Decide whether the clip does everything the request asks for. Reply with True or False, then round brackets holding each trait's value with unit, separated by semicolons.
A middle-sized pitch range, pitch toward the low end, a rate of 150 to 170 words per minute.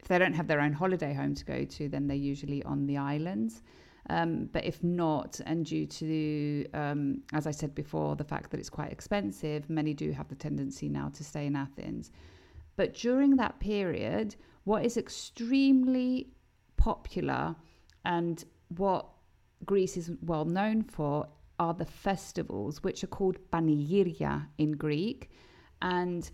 False (4.9 semitones; 155 Hz; 160 wpm)